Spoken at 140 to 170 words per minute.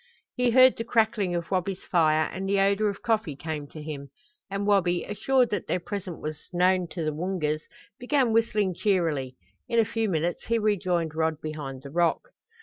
No: average, 185 wpm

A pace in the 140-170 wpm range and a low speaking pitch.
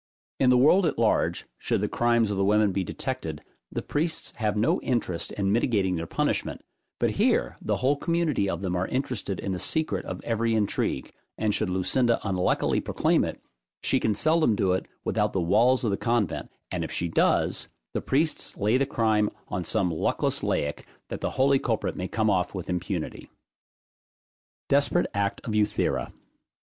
No: average, 180 wpm; low, 105 Hz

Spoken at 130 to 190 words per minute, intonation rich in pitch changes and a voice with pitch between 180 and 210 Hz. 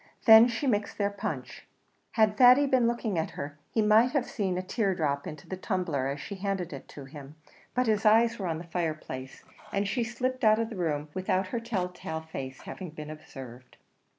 No: fast, 205 wpm; wide, 6.4 semitones; high, 190 Hz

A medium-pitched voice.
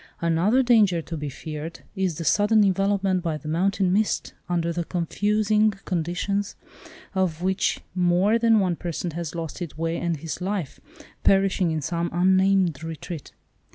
Yes: medium, 180 Hz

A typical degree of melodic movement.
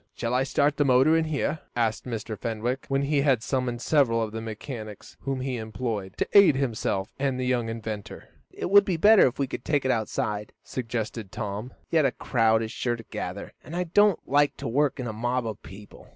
Yes: average, 4.0 semitones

